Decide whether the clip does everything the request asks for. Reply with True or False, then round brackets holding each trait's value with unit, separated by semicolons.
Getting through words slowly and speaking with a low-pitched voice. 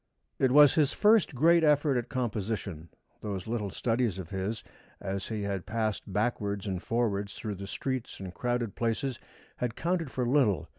False (165 wpm; 115 Hz)